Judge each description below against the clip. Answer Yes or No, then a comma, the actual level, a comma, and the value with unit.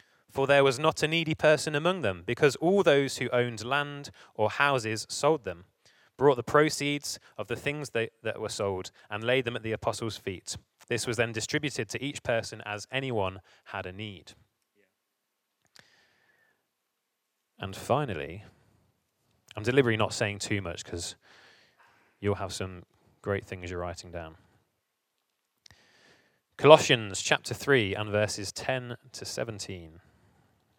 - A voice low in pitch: Yes, low, 115 Hz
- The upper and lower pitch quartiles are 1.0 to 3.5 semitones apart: No, average, 5.3 semitones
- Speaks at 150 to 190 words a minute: No, average, 140 wpm